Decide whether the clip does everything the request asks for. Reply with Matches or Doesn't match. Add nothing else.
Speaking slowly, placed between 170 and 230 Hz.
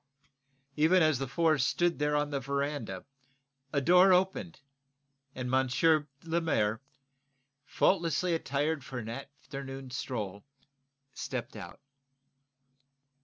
Doesn't match